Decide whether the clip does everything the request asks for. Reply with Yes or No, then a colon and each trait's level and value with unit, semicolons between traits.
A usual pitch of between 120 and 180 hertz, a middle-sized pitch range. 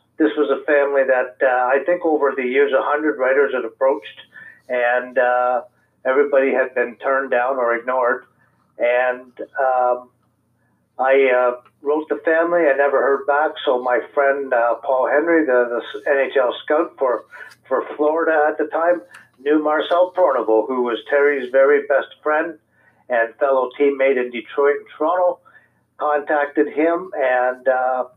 Yes: medium, 140 Hz; average, 3.2 semitones